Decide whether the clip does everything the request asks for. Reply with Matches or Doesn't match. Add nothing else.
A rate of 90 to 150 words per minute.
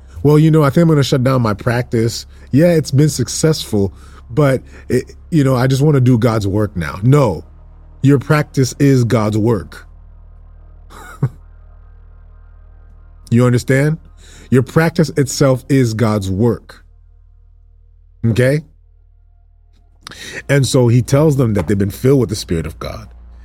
Matches